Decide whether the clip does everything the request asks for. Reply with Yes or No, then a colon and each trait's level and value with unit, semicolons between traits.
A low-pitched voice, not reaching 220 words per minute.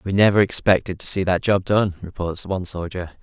Yes: very low, 95 Hz; fast, 205 wpm